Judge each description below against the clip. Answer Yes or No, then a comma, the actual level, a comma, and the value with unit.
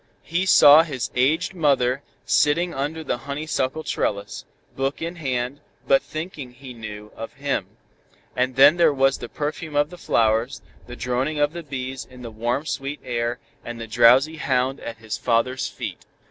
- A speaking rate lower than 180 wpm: Yes, average, 170 wpm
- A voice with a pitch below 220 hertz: Yes, low, 135 Hz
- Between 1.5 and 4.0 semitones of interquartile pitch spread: Yes, average, 3.6 semitones